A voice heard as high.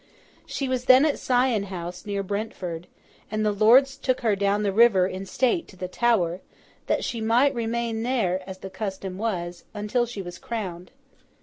Yes: high, 210 Hz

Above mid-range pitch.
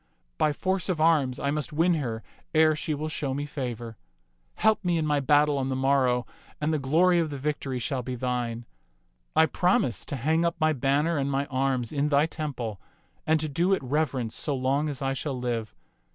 No: medium, 145 Hz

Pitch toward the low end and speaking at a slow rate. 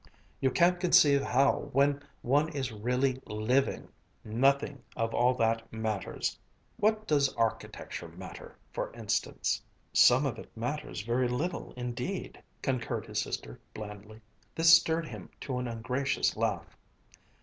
Yes: low, 130 Hz; slow, 130 wpm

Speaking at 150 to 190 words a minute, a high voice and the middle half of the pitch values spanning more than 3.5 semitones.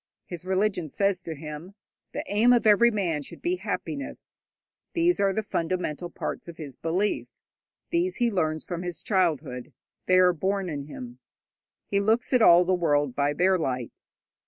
No: average, 170 wpm; medium, 180 Hz; average, 4.6 semitones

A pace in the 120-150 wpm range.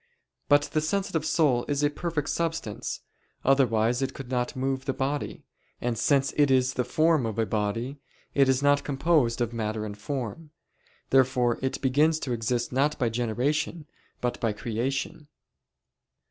No: average, 160 wpm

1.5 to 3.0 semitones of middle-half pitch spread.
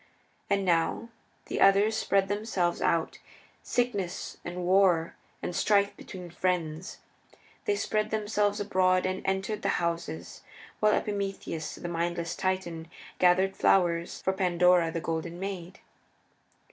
Yes: narrow, 2.6 semitones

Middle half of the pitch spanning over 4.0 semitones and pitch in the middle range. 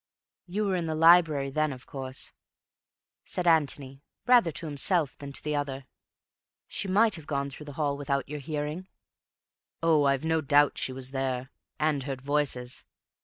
No: average, 2.9 semitones; medium, 145 Hz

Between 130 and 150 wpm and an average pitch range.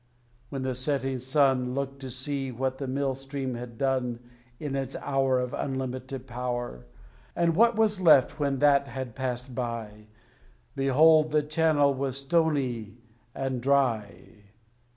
No: average, 140 wpm; narrow, 2.0 semitones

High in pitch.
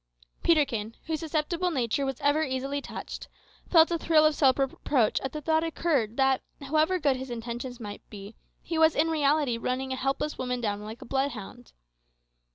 Yes: very high, 270 Hz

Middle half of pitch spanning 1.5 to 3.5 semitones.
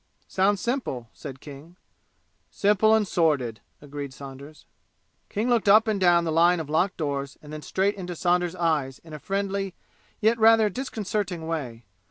No: wide, 5.5 semitones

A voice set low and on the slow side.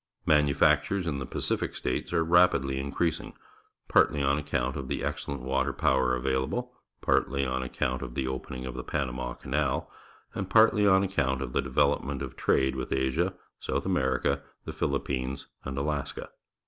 No: very low, 70 Hz; average, 160 wpm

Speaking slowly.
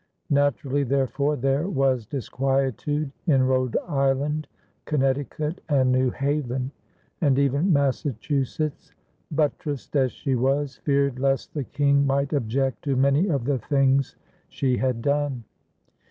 Yes: slow, 125 wpm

